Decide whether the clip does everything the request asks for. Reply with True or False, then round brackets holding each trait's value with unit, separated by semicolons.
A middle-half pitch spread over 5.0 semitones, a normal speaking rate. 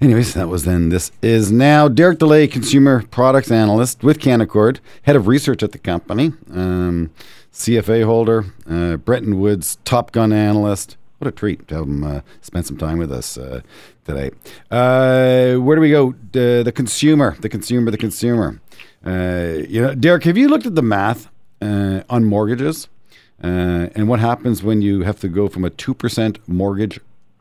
True (5.6 semitones; 180 wpm)